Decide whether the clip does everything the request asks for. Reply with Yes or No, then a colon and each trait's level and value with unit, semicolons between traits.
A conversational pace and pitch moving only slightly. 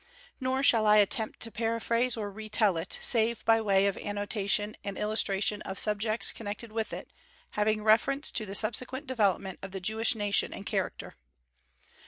Yes: average, 170 wpm; narrow, 2.0 semitones